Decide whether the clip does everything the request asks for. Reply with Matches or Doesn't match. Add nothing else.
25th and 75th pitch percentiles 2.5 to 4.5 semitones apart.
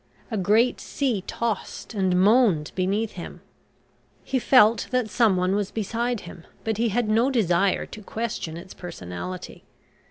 Matches